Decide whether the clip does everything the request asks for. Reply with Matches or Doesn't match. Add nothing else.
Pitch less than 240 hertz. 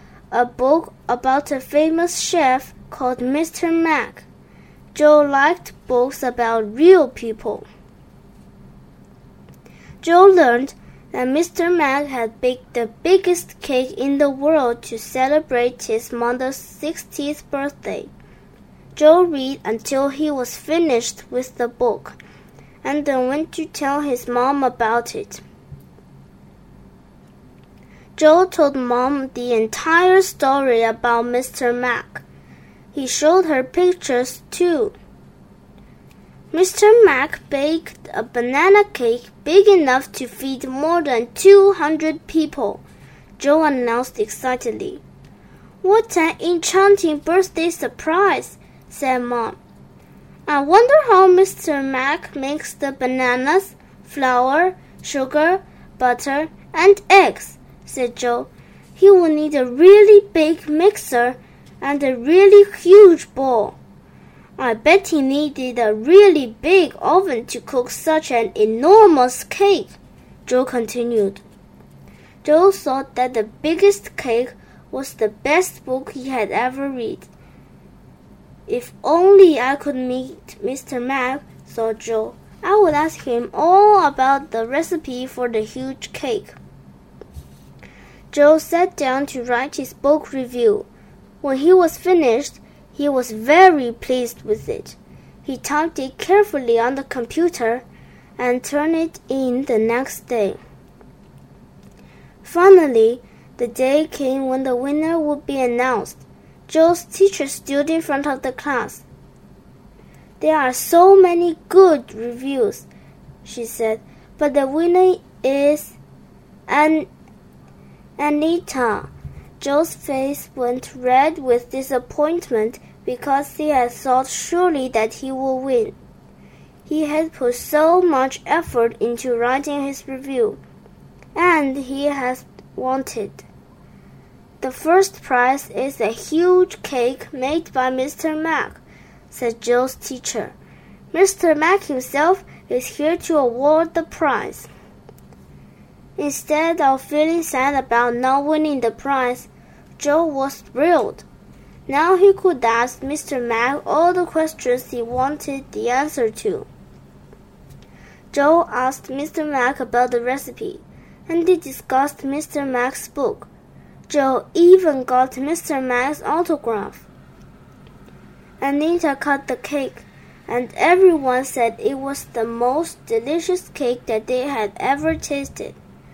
Doesn't match